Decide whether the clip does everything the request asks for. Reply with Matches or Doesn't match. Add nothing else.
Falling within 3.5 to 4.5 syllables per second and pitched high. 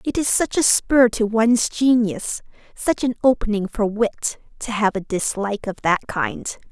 Matches